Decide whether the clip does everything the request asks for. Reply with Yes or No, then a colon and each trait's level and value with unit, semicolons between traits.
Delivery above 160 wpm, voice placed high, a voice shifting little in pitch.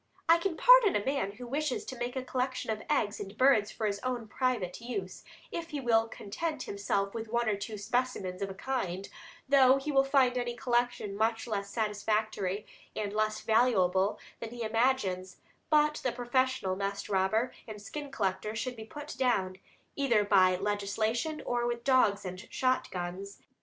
No: average, 175 wpm; high, 225 Hz; average, 4.3 semitones